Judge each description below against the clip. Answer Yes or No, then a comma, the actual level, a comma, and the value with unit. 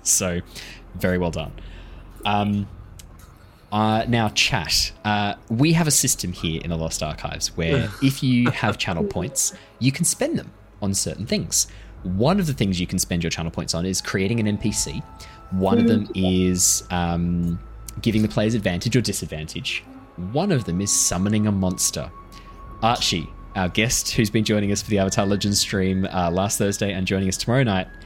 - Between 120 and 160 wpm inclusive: No, average, 180 wpm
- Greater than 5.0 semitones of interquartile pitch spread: No, average, 3.4 semitones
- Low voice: Yes, low, 100 Hz